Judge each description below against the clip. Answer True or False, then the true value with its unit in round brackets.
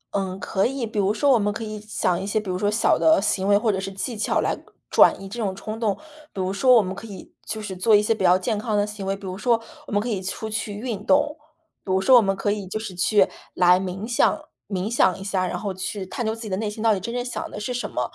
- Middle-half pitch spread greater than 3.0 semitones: False (2.7 semitones)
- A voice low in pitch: False (205 Hz)